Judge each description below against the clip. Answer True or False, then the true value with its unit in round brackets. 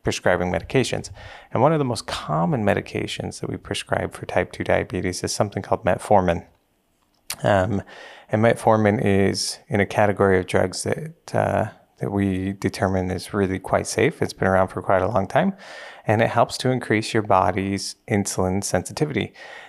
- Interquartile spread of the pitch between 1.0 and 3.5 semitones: True (2.6 semitones)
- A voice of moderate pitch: False (100 Hz)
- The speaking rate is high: False (170 wpm)